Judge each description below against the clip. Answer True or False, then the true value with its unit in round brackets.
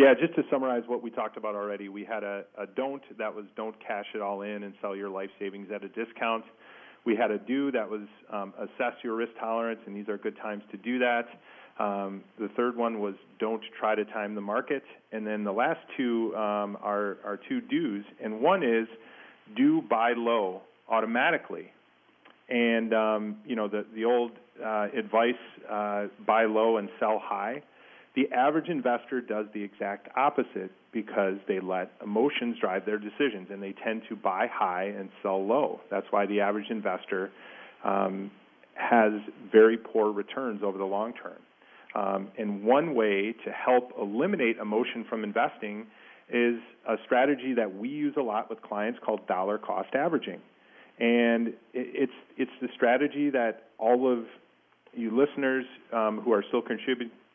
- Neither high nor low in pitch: False (110 Hz)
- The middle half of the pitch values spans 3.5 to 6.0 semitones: False (2.6 semitones)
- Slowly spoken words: False (175 wpm)